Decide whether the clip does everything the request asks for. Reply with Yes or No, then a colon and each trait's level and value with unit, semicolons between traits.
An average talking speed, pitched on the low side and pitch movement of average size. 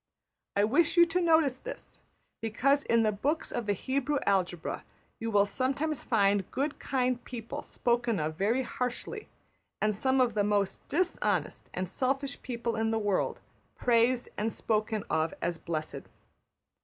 No: average, 155 wpm; high, 235 Hz; average, 4.6 semitones